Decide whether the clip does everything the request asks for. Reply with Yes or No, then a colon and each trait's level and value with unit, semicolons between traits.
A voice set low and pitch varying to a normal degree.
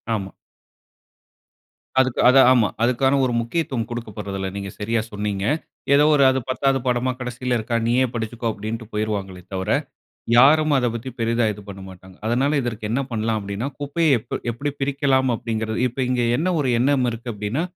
Yes: low, 120 Hz; average, 3.7 semitones